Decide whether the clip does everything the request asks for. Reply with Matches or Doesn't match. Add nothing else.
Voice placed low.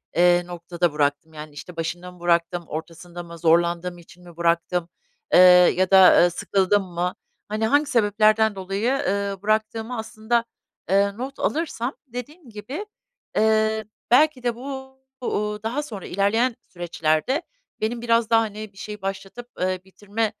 Doesn't match